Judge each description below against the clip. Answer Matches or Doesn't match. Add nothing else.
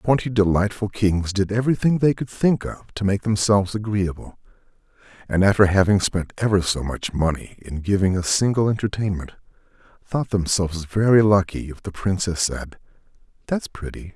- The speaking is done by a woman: Doesn't match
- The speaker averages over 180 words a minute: Doesn't match